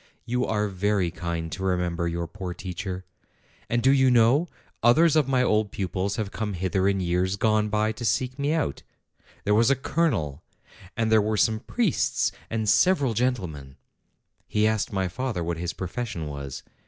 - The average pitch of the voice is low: Yes, low, 105 Hz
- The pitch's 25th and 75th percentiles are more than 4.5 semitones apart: Yes, average, 5.0 semitones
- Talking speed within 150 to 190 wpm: Yes, average, 175 wpm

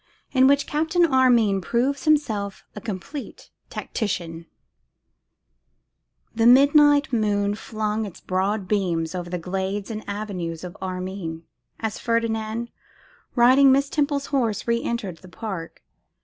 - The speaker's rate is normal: No, slow, 120 wpm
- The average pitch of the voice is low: No, high, 215 Hz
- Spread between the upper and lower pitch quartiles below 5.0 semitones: No, wide, 5.5 semitones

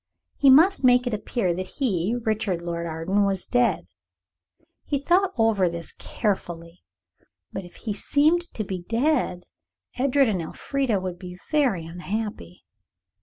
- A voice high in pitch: Yes, high, 205 Hz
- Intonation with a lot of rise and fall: Yes, wide, 6.3 semitones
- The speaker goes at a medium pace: Yes, average, 145 wpm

